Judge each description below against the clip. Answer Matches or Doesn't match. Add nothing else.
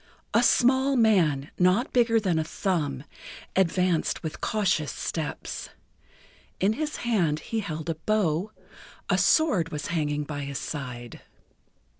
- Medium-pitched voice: Matches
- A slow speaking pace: Matches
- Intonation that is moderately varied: Doesn't match